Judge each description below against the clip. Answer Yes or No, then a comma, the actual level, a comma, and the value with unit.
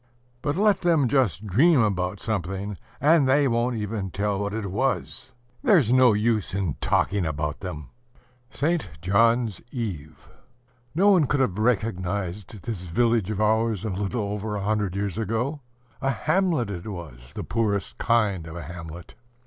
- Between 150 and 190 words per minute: Yes, average, 155 wpm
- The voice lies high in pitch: No, low, 105 Hz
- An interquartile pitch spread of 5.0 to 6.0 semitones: No, average, 4.6 semitones